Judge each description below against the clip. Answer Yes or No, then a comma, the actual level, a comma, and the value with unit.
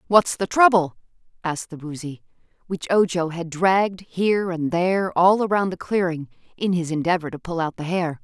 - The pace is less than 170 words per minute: No, average, 180 wpm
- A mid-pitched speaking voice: Yes, medium, 175 Hz